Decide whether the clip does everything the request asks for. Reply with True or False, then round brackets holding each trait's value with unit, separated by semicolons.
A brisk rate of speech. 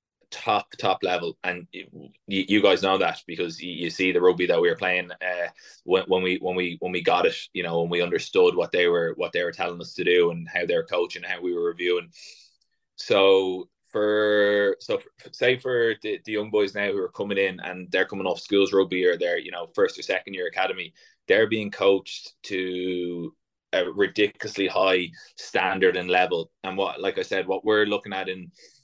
True (210 wpm)